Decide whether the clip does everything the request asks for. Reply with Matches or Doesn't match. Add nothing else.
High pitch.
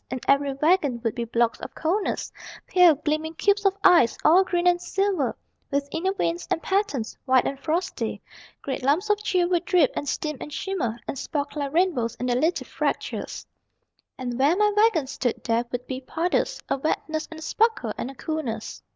Matches